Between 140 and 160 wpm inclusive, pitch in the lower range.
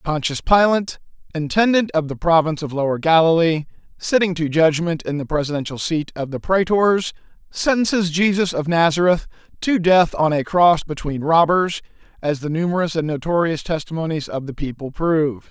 No: average, 155 wpm; medium, 165 Hz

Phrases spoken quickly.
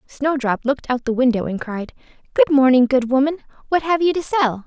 Yes: fast, 220 wpm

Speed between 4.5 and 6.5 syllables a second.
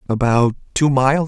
Yes: 5.2 syllables/s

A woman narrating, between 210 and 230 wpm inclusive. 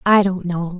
Yes: female; fast, 225 wpm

